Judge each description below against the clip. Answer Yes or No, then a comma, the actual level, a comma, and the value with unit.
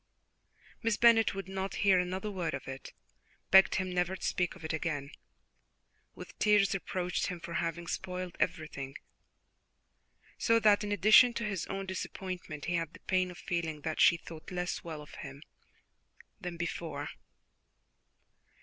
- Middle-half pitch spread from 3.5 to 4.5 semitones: No, average, 2.8 semitones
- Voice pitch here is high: No, medium, 180 Hz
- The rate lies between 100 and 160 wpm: Yes, average, 155 wpm